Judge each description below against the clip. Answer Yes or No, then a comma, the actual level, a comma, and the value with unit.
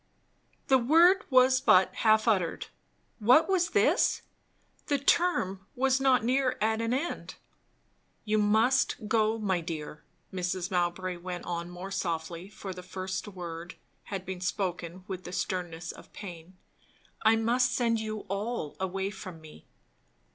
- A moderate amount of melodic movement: Yes, average, 4.8 semitones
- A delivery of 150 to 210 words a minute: No, average, 140 wpm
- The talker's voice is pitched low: No, high, 195 Hz